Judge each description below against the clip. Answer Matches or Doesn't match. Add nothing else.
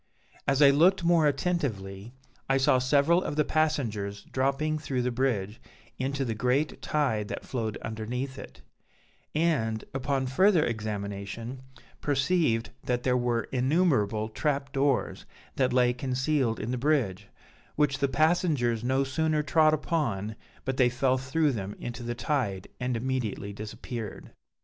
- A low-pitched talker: Matches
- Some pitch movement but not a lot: Matches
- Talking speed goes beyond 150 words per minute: Doesn't match